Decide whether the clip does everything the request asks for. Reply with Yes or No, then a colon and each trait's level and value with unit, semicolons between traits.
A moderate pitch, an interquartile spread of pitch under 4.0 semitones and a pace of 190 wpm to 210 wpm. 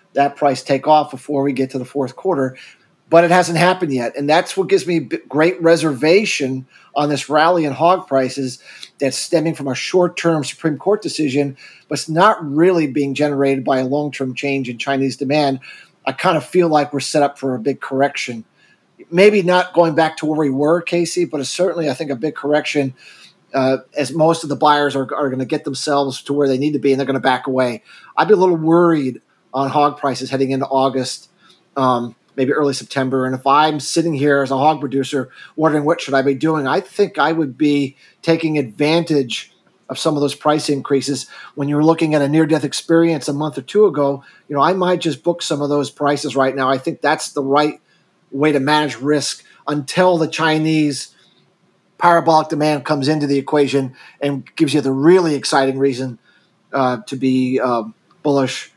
Yes: medium, 145 Hz; average, 2.9 semitones; fast, 205 wpm